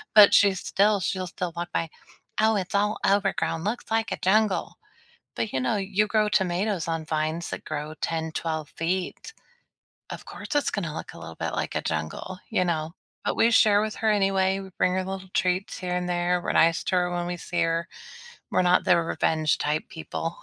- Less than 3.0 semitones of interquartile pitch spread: No, average, 3.3 semitones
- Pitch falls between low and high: Yes, medium, 180 Hz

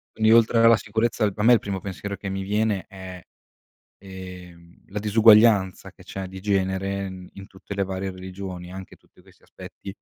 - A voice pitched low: Yes, very low, 95 Hz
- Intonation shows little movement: Yes, narrow, 2.0 semitones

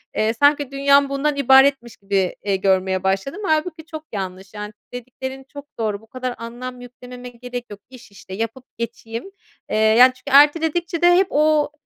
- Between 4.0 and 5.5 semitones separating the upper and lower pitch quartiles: Yes, average, 4.7 semitones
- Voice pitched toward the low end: No, very high, 250 Hz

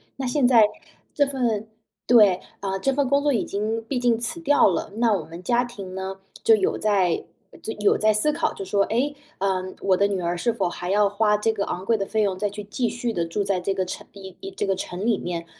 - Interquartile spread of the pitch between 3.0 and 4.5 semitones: Yes, average, 3.8 semitones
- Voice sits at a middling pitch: No, high, 210 Hz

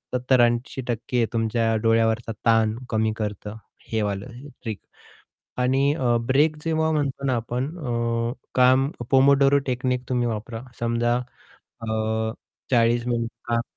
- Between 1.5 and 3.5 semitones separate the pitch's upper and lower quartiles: Yes, narrow, 2.5 semitones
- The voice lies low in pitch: Yes, low, 120 Hz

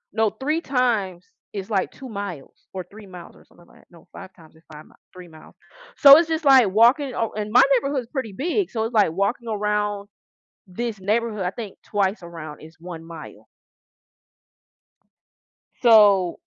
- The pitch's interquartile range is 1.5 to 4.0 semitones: No, average, 4.8 semitones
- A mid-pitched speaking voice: No, high, 210 Hz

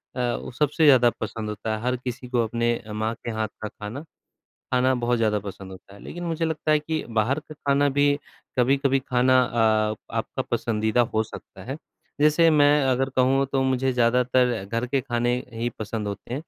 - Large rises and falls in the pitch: No, average, 3.5 semitones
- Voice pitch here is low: Yes, low, 125 Hz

